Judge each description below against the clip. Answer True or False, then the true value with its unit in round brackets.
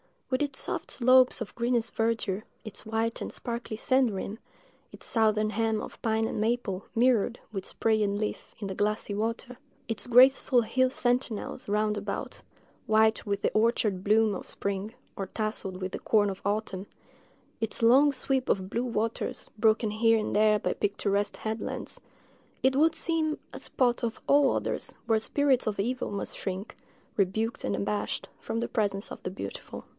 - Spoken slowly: False (160 wpm)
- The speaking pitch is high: True (220 Hz)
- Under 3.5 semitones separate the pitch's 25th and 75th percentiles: True (2.8 semitones)